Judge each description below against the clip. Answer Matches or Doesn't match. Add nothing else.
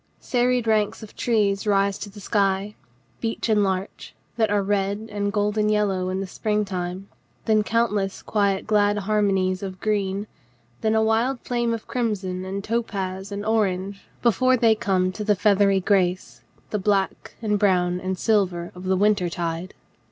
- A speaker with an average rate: Matches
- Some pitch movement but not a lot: Doesn't match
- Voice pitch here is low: Doesn't match